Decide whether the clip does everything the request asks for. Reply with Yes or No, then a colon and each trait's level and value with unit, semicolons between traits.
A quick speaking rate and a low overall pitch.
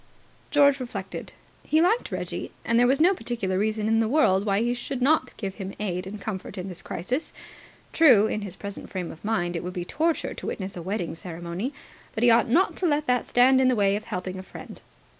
No: fast, 225 wpm; high, 215 Hz